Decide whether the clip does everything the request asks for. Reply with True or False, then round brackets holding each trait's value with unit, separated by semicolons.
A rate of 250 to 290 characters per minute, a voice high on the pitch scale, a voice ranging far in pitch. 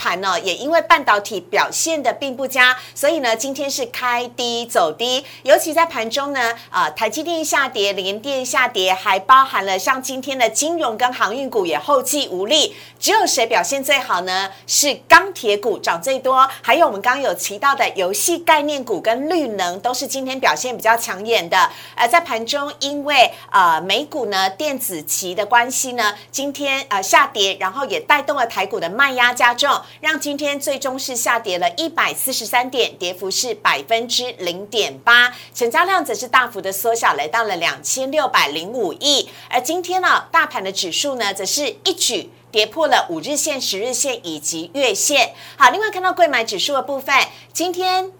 False (285 characters per minute; 265 Hz; 5.0 semitones)